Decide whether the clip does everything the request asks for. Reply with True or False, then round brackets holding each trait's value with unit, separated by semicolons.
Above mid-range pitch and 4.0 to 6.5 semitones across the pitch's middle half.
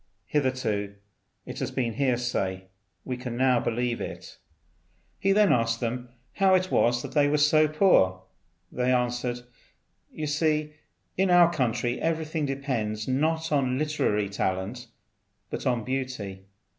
False (130 Hz; 4.5 semitones)